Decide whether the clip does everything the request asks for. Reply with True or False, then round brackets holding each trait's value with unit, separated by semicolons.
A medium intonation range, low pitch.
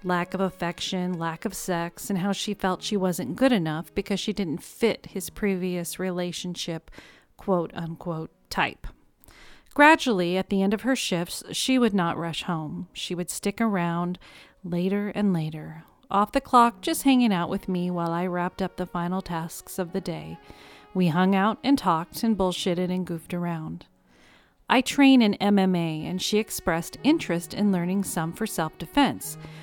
False (3.0 semitones; 185 Hz)